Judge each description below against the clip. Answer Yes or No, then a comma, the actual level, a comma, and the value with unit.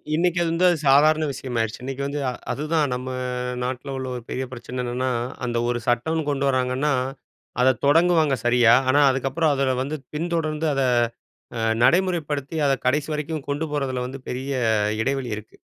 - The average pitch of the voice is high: No, low, 135 Hz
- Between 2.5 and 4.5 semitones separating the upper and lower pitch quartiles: Yes, average, 3.3 semitones